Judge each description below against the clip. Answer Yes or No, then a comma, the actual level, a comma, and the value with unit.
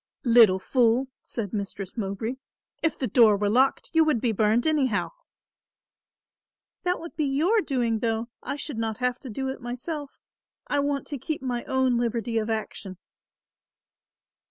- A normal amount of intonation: Yes, average, 3.8 semitones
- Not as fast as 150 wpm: No, average, 155 wpm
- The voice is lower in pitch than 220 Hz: No, high, 245 Hz